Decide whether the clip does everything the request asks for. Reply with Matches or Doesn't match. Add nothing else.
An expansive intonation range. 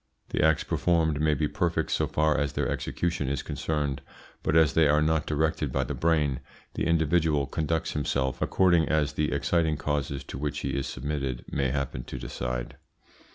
Doesn't match